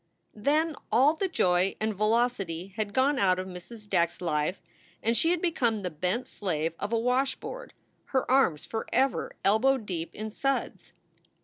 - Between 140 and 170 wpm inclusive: Yes, average, 165 wpm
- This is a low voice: No, high, 220 Hz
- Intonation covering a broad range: Yes, wide, 6.2 semitones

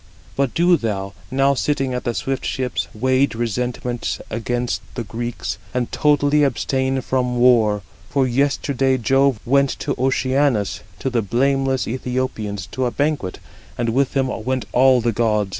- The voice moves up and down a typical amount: No, narrow, 2.3 semitones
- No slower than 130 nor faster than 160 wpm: Yes, average, 155 wpm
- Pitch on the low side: Yes, low, 125 Hz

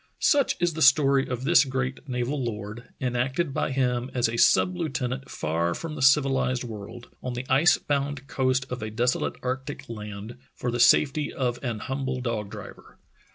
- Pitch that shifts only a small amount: Yes, narrow, 2.2 semitones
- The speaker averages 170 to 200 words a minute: Yes, average, 175 wpm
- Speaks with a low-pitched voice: Yes, low, 130 Hz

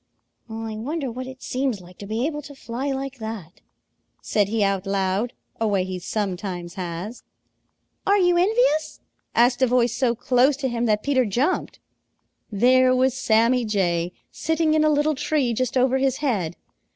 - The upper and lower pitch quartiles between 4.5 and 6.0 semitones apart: Yes, average, 4.8 semitones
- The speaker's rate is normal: Yes, average, 170 wpm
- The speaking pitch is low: No, high, 245 Hz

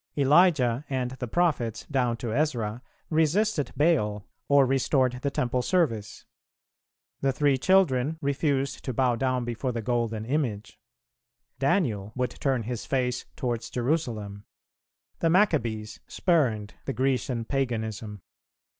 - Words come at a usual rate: No, slow, 120 wpm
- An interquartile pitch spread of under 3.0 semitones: No, average, 3.7 semitones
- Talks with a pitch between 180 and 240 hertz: No, low, 125 Hz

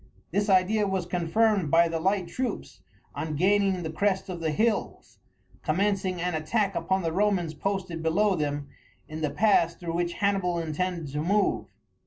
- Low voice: No, medium, 180 Hz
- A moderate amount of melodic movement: Yes, average, 3.5 semitones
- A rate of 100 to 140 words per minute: No, average, 165 wpm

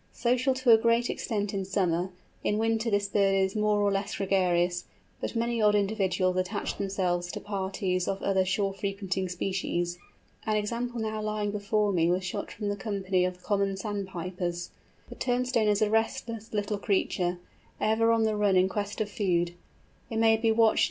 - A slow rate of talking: No, average, 165 wpm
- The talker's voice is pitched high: Yes, high, 200 Hz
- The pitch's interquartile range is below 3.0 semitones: Yes, narrow, 2.6 semitones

